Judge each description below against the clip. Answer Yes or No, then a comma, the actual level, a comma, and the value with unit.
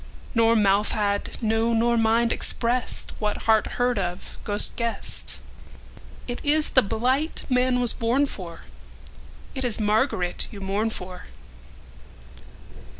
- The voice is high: Yes, high, 225 Hz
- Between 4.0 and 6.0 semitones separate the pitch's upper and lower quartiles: No, average, 3.0 semitones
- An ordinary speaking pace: No, slow, 110 wpm